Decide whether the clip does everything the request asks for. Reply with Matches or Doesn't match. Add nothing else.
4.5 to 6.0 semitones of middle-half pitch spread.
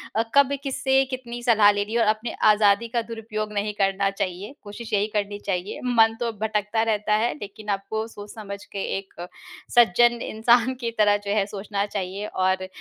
Doesn't match